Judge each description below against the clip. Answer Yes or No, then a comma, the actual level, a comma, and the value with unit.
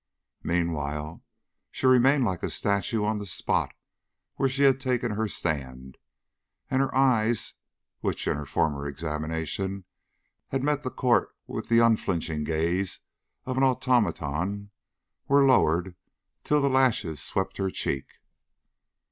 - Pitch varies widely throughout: Yes, wide, 8.0 semitones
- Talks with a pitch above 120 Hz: No, low, 100 Hz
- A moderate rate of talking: No, slow, 130 wpm